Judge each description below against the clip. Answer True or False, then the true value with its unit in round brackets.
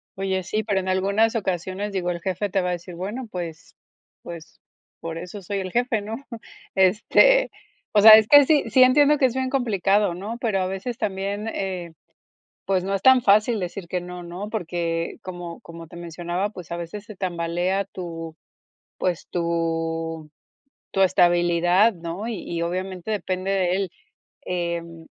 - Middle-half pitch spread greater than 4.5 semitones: False (3.2 semitones)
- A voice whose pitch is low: False (185 Hz)